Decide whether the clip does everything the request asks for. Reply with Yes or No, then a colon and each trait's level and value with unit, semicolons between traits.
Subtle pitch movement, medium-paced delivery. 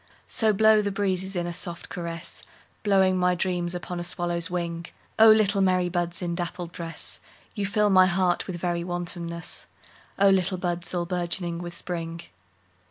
Yes: narrow, 1.8 semitones; average, 150 wpm